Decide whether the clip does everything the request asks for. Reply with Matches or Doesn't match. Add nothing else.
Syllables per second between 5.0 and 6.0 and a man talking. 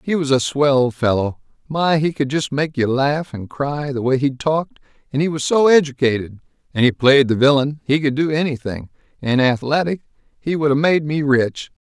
Matches